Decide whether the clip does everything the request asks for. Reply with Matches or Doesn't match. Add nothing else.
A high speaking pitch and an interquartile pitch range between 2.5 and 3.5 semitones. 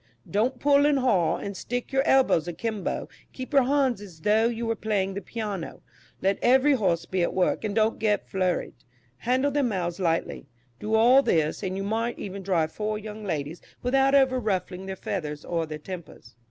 Doesn't match